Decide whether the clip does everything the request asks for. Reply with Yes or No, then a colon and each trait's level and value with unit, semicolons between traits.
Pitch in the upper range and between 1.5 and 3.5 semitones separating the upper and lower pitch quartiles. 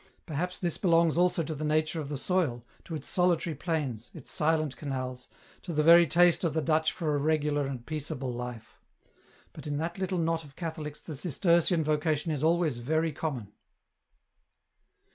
No: medium, 155 Hz; average, 2.7 semitones